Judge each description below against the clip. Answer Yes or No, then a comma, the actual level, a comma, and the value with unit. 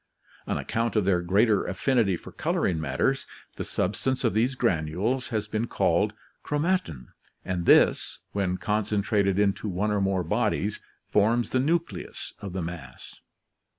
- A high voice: No, low, 105 Hz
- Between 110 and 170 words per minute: Yes, average, 145 wpm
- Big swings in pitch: No, average, 4.1 semitones